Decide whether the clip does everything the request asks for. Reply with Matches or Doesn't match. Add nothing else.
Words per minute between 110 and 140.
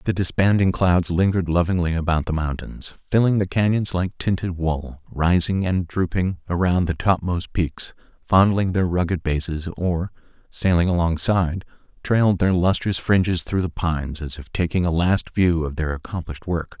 Doesn't match